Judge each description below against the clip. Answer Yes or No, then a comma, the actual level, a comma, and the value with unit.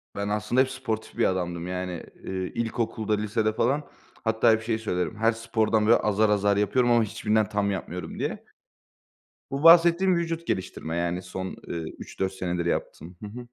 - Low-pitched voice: Yes, low, 110 Hz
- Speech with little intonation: No, average, 3.8 semitones